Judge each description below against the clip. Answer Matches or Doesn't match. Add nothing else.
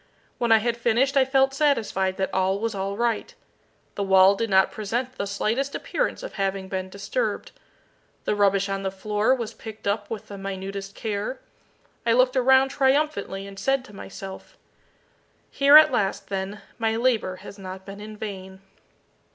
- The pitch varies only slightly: Doesn't match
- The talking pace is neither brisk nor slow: Matches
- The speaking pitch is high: Matches